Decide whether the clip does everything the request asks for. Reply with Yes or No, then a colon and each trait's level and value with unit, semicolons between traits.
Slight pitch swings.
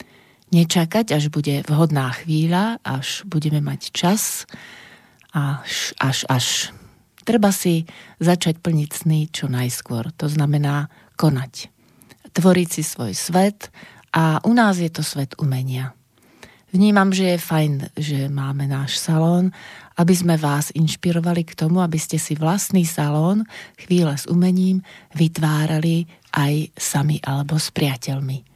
No: average, 3.6 semitones